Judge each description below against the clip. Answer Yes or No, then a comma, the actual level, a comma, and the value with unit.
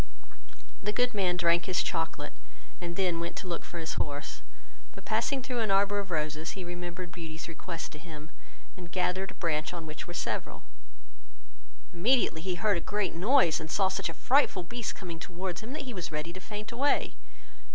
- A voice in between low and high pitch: Yes, medium, 175 Hz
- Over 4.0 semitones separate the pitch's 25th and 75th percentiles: No, average, 3.4 semitones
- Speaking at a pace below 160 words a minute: No, average, 195 wpm